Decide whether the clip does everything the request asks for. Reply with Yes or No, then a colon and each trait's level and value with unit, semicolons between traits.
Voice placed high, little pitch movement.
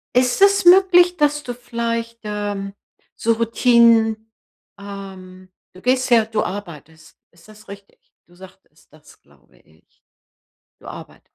No: high, 220 Hz; average, 4.3 semitones